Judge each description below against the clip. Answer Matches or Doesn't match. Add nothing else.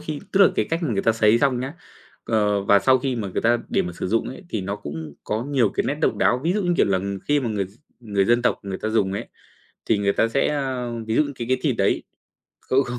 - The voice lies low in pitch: Matches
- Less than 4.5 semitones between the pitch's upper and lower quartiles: Doesn't match